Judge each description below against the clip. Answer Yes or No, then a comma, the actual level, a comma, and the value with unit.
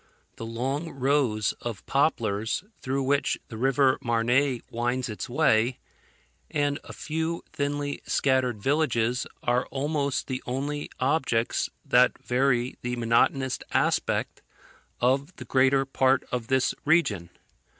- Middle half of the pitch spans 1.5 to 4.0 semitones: Yes, average, 2.9 semitones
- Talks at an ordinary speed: No, slow, 120 wpm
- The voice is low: Yes, low, 130 Hz